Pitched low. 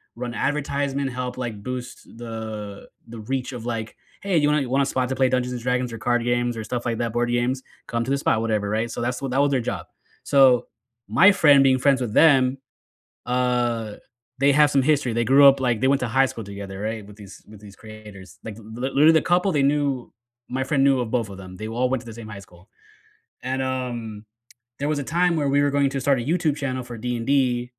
Yes: low, 125 Hz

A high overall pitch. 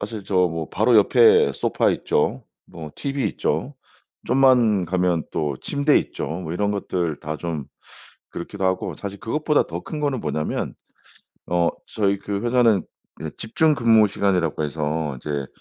No: low, 100 Hz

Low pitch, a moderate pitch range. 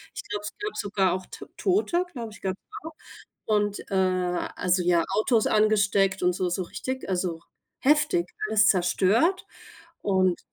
No: high, 195 Hz; average, 3.1 semitones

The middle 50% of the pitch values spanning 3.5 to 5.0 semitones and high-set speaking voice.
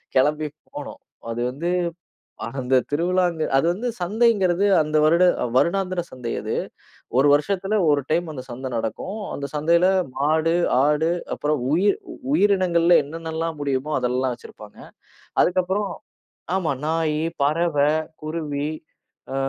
No: average, 3.8 semitones; medium, 160 Hz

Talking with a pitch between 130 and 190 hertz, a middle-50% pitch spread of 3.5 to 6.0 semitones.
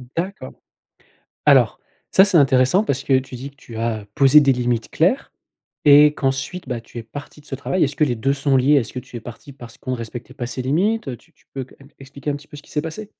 No: low, 135 Hz; average, 3.0 semitones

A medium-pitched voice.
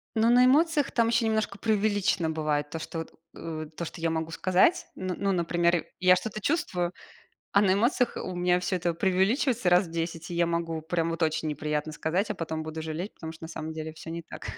Yes: medium, 175 Hz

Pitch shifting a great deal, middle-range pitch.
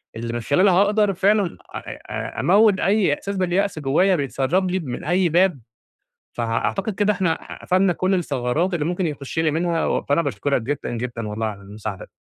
Yes: wide, 6.0 semitones; medium, 170 Hz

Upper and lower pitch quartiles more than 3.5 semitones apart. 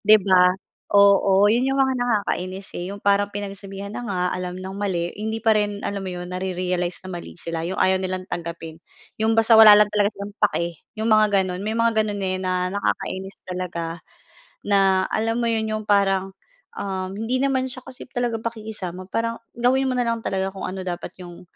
No: average, 2.9 semitones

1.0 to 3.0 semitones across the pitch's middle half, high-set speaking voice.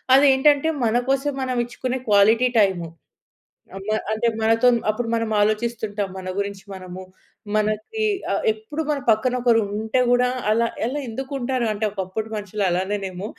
No: average, 3.7 semitones; high, 220 Hz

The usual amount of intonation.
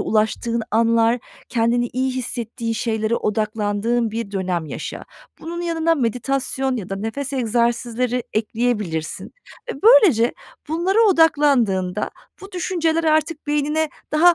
No: wide, 5.7 semitones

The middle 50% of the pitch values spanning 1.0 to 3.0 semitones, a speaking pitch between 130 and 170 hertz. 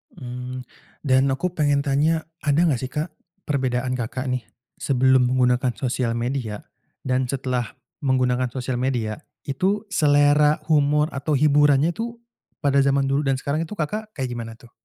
Yes: average, 2.7 semitones; low, 135 Hz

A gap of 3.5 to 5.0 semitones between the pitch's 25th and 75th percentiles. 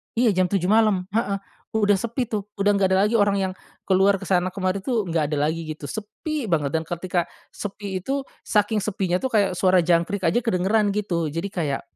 No: average, 3.0 semitones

